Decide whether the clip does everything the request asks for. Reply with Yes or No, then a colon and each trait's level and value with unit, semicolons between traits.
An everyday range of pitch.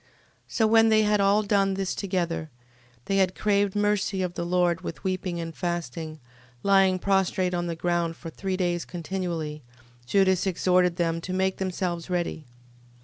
No: narrow, 2.2 semitones